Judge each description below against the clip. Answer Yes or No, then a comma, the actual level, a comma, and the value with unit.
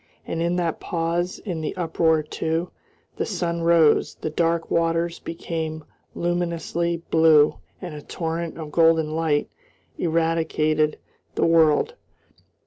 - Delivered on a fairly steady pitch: Yes, narrow, 1.1 semitones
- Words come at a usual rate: No, slow, 125 wpm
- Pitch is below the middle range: No, medium, 165 Hz